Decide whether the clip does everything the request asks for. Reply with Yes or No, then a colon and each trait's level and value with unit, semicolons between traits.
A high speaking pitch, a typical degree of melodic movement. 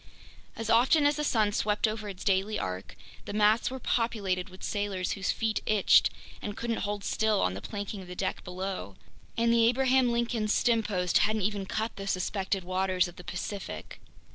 Yes: high, 205 Hz; average, 3.2 semitones